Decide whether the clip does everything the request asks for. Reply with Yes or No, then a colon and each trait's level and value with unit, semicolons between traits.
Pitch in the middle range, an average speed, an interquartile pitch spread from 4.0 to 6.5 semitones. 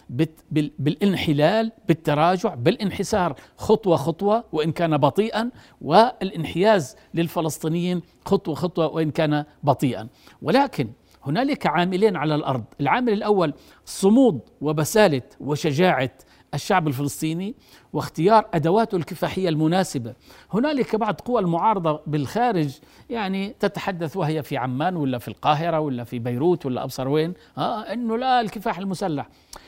Yes: medium, 170 Hz; average, 110 wpm; average, 5.2 semitones